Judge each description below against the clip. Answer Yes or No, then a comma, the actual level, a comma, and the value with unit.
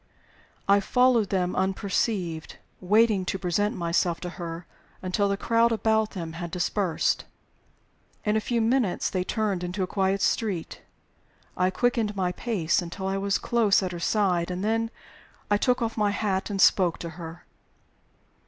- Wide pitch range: No, average, 3.4 semitones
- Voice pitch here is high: Yes, high, 195 Hz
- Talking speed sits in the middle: Yes, average, 160 wpm